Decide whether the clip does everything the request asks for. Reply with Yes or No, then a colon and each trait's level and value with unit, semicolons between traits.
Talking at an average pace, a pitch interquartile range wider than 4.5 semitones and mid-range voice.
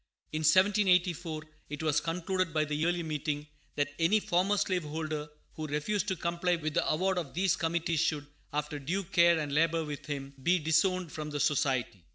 No: average, 185 wpm; average, 3.1 semitones; medium, 160 Hz